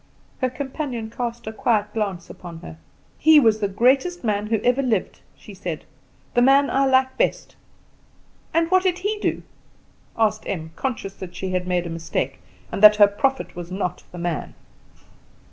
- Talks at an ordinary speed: Yes, average, 175 wpm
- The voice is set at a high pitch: Yes, high, 220 Hz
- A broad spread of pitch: Yes, wide, 6.3 semitones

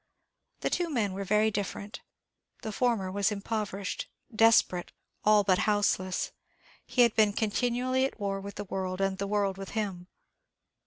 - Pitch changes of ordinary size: No, narrow, 2.1 semitones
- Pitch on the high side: Yes, high, 205 Hz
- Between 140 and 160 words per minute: Yes, average, 155 wpm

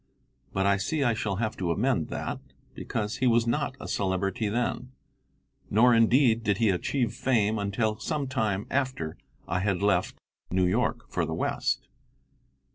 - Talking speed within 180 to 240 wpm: No, average, 160 wpm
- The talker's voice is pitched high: No, low, 110 Hz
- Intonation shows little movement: No, average, 3.8 semitones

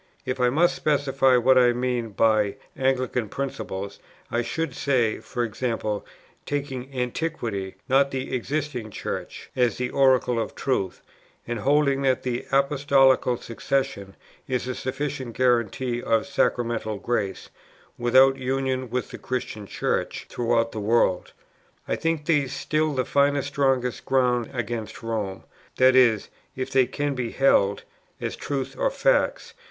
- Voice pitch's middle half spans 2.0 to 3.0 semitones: Yes, average, 2.7 semitones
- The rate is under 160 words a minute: Yes, slow, 135 wpm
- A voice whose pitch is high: No, low, 130 Hz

